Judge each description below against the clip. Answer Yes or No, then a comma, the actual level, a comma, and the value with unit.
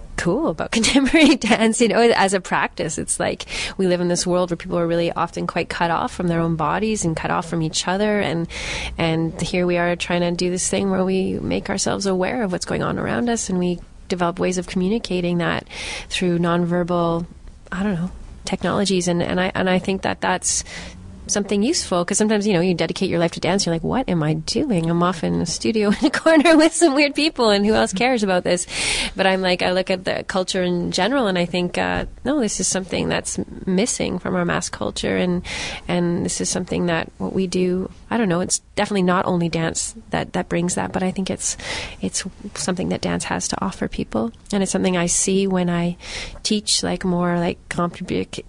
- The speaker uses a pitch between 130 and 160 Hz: No, medium, 185 Hz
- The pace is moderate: No, fast, 225 wpm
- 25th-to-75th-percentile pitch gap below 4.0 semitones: Yes, average, 2.8 semitones